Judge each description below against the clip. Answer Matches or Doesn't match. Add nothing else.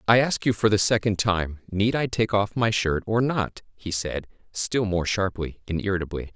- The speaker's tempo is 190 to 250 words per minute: Matches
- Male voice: Matches